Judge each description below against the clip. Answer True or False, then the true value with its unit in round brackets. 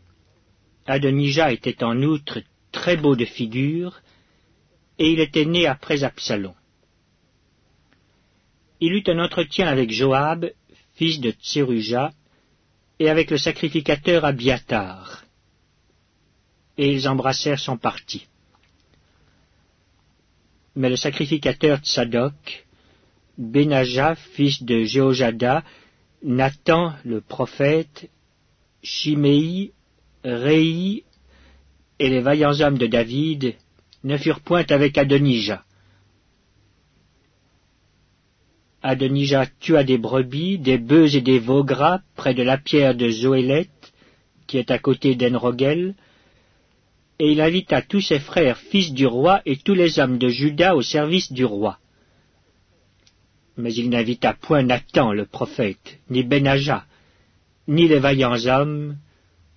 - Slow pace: True (110 wpm)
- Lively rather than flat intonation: False (4.4 semitones)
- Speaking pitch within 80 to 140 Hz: True (135 Hz)